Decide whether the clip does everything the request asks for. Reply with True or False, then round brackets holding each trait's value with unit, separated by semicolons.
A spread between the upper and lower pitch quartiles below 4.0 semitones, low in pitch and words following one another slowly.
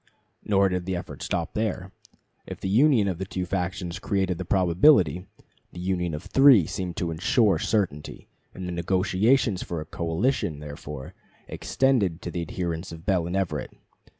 False (2.6 semitones; 90 Hz; 165 wpm)